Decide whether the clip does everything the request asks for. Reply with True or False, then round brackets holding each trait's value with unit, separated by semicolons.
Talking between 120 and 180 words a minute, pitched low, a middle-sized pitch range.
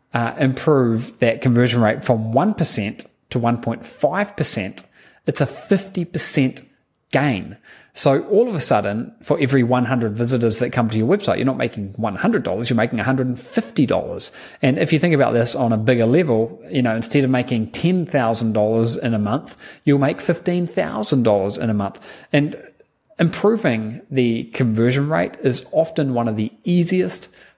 True (150 wpm; 125 Hz; 4.8 semitones)